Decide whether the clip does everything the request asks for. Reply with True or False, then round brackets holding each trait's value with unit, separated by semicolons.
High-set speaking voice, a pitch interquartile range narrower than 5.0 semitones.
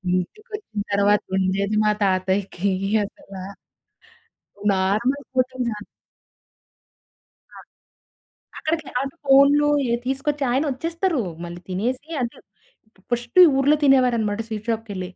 False (235 Hz; 5.5 semitones)